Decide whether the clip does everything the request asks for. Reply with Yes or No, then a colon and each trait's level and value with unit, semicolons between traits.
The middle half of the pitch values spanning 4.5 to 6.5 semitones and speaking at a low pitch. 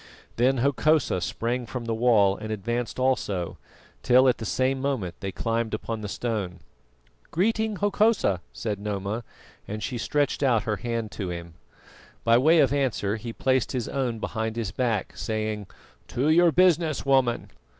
No: average, 3.9 semitones; low, 120 Hz